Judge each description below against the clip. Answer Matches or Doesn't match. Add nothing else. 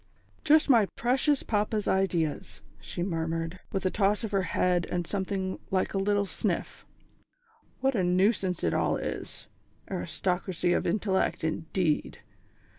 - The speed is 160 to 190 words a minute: Doesn't match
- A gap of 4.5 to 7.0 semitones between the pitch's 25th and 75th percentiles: Doesn't match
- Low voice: Doesn't match